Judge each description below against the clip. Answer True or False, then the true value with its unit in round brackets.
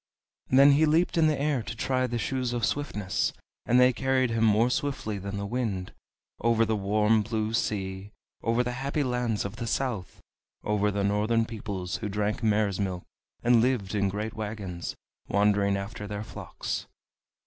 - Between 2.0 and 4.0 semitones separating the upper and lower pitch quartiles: True (3.4 semitones)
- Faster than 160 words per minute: True (170 wpm)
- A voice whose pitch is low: True (110 Hz)